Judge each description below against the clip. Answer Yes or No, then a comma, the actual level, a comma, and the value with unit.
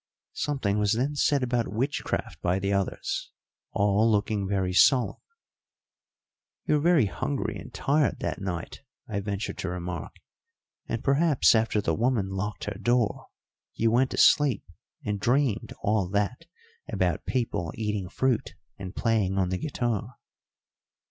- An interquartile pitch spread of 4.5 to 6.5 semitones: Yes, average, 4.8 semitones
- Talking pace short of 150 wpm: Yes, average, 140 wpm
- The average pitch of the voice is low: Yes, low, 110 Hz